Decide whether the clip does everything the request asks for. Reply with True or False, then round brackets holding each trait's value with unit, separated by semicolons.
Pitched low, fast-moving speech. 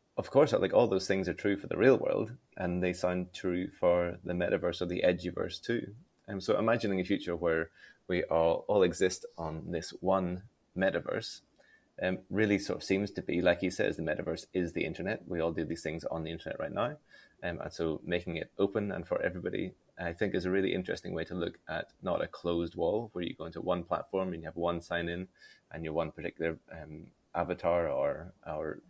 True (90 Hz; 220 wpm)